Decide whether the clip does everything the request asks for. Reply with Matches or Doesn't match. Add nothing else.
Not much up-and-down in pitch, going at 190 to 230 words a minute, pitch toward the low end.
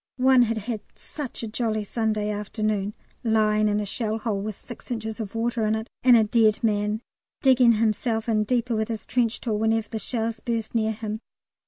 Doesn't match